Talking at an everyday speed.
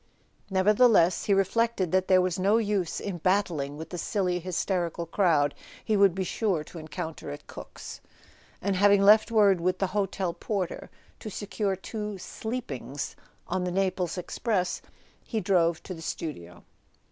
Yes: average, 155 wpm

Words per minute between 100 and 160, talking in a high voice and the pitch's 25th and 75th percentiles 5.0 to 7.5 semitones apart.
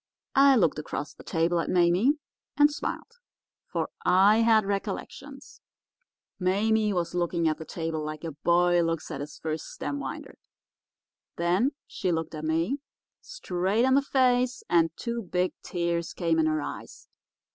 No: average, 155 wpm; medium, 175 Hz; average, 5.3 semitones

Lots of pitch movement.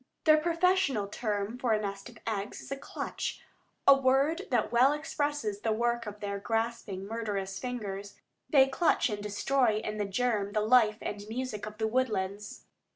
No: average, 4.0 semitones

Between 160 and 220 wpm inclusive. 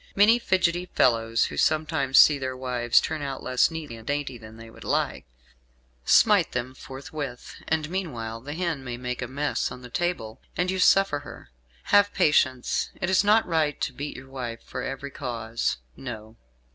Yes: average, 180 wpm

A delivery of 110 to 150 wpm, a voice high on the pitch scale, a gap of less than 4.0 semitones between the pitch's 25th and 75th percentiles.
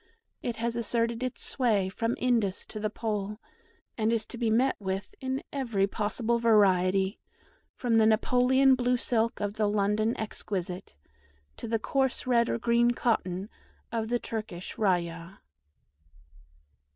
Yes: average, 140 wpm; high, 225 Hz; average, 2.9 semitones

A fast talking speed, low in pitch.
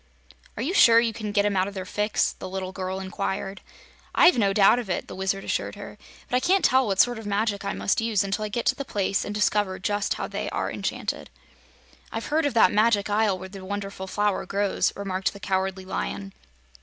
No: fast, 225 wpm; high, 200 Hz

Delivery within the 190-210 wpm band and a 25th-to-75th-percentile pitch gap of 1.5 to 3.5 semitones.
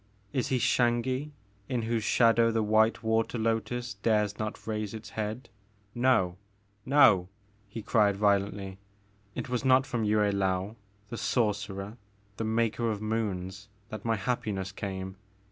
No: average, 145 wpm; narrow, 2.5 semitones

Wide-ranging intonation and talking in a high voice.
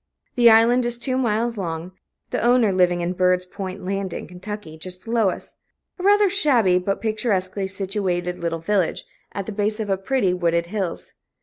No: average, 3.9 semitones; high, 195 Hz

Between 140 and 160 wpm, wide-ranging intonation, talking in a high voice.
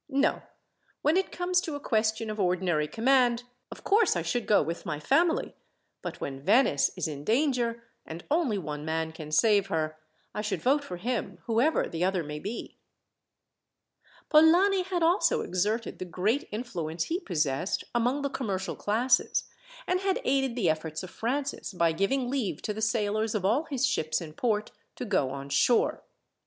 No: average, 175 wpm; wide, 7.9 semitones; high, 220 Hz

